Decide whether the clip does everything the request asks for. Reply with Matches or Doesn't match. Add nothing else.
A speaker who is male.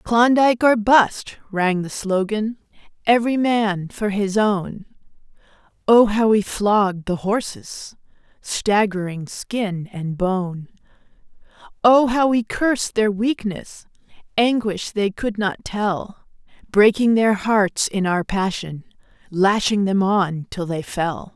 Doesn't match